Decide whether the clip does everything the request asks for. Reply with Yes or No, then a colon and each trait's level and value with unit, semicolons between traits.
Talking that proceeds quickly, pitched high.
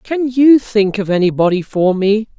No: average, 175 wpm; high, 215 Hz